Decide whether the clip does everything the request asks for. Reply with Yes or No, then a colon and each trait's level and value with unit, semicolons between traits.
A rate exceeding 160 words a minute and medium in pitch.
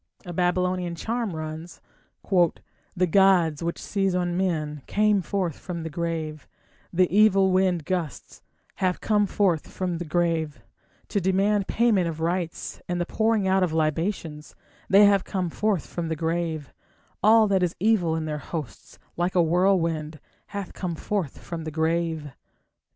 No: average, 155 wpm; medium, 175 Hz